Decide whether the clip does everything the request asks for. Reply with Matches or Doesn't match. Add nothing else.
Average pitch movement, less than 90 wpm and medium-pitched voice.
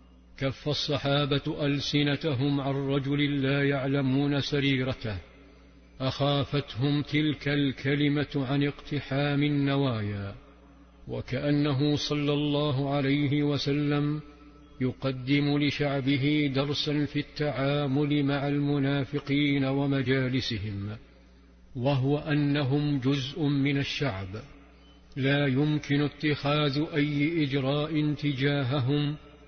Doesn't match